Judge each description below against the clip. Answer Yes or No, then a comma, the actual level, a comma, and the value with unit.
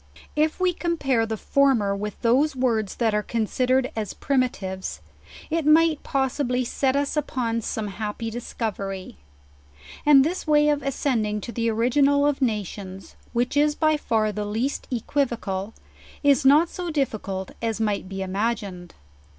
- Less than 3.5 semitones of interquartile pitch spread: No, average, 5.2 semitones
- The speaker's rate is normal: Yes, average, 150 wpm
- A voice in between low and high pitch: No, high, 240 Hz